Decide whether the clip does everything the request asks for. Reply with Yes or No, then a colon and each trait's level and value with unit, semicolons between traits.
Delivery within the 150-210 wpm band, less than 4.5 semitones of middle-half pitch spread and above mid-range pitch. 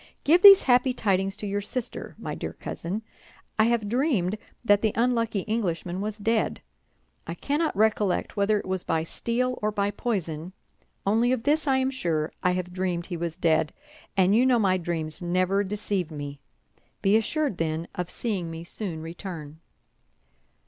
No: average, 170 wpm; average, 4.9 semitones; high, 200 Hz